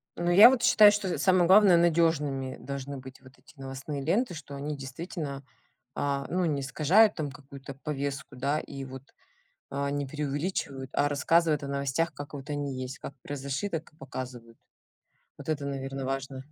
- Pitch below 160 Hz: Yes, medium, 140 Hz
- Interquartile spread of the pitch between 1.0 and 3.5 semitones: Yes, average, 3.2 semitones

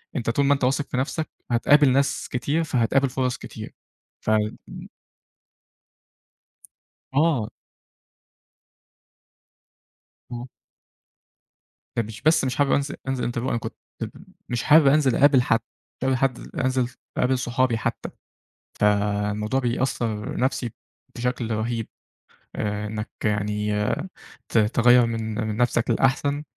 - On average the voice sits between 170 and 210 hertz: No, low, 125 Hz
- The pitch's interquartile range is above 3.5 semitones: No, average, 3.2 semitones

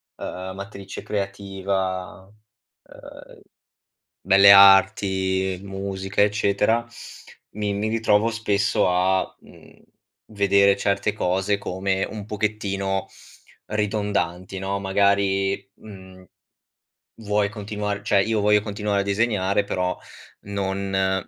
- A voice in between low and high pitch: No, low, 100 Hz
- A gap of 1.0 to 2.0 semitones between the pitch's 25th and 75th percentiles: Yes, narrow, 1.3 semitones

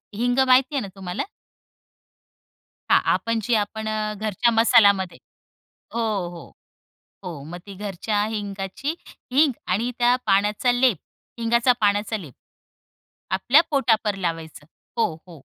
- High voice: Yes, high, 210 Hz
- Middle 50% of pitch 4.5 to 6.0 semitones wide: No, average, 3.7 semitones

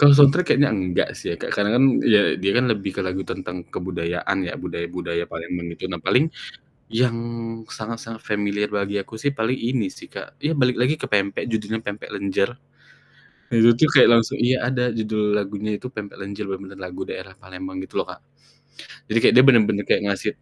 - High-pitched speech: No, low, 105 Hz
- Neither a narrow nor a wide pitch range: Yes, average, 4.0 semitones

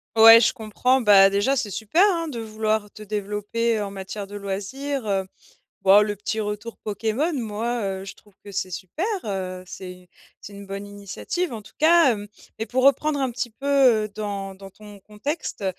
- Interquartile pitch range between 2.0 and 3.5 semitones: Yes, average, 2.8 semitones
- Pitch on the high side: Yes, high, 210 Hz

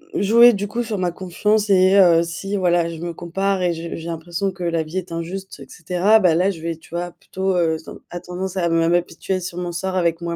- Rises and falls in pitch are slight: Yes, narrow, 2.3 semitones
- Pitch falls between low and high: Yes, medium, 175 Hz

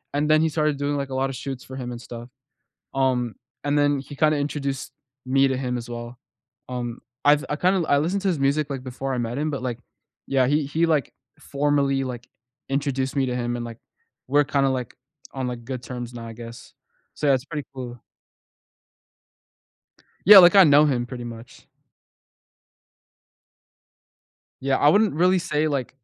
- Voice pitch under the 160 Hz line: Yes, low, 135 Hz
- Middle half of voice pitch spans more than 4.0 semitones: No, average, 2.9 semitones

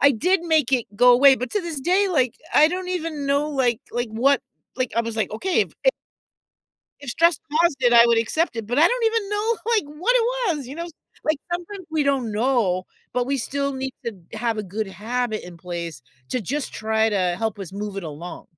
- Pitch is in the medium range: No, very high, 260 Hz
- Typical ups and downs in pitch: No, wide, 6.9 semitones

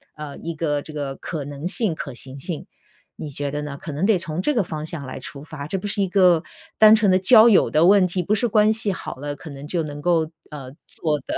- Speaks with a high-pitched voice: No, medium, 160 Hz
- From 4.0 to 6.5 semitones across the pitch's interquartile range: Yes, average, 4.8 semitones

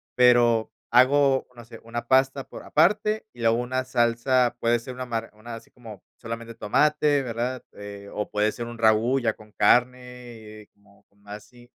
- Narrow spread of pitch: Yes, narrow, 2.3 semitones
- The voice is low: Yes, low, 120 Hz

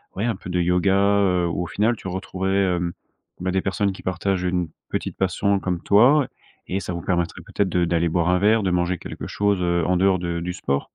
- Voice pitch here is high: No, very low, 90 Hz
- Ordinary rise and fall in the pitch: No, narrow, 2.0 semitones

